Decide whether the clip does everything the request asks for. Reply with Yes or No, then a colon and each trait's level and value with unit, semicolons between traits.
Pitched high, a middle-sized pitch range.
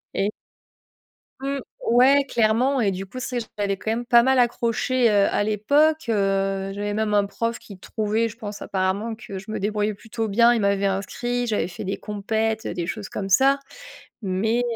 Yes: high, 215 Hz; average, 3.1 semitones